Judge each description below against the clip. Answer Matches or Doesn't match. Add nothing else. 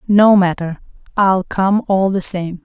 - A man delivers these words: Doesn't match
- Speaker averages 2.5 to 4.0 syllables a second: Matches